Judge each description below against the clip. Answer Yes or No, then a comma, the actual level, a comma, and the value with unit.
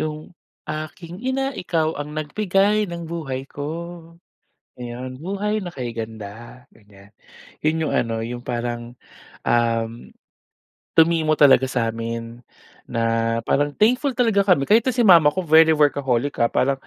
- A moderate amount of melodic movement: No, wide, 6.6 semitones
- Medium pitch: Yes, medium, 150 Hz